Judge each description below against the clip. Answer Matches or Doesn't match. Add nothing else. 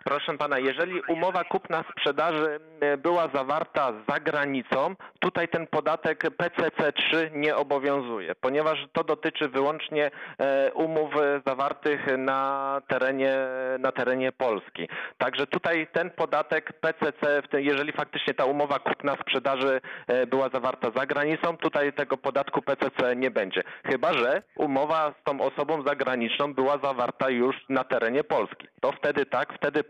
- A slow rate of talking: Doesn't match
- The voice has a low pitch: Doesn't match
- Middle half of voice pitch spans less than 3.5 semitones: Matches